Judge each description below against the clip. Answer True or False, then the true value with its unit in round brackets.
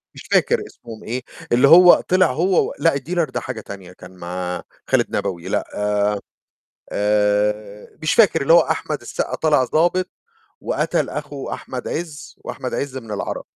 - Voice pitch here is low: True (130 Hz)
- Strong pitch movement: True (7.8 semitones)